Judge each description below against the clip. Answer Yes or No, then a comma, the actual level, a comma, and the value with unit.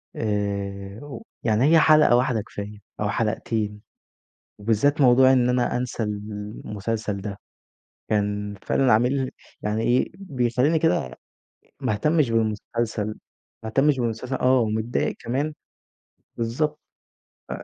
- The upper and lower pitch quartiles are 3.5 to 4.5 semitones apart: Yes, average, 3.8 semitones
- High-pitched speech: No, low, 115 Hz